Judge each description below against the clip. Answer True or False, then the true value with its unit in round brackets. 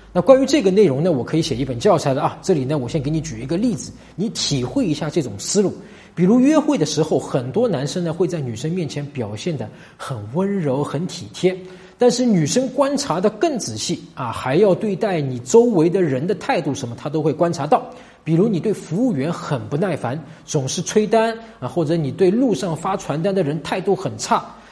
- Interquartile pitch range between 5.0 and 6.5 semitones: True (5.6 semitones)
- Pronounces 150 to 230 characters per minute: False (310 characters per minute)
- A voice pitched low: False (170 Hz)